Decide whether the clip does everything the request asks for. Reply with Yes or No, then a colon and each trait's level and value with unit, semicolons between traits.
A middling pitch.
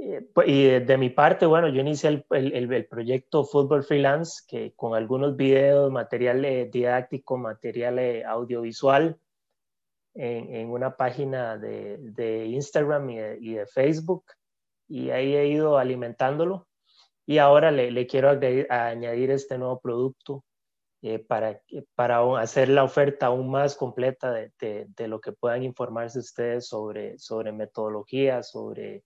No: low, 130 Hz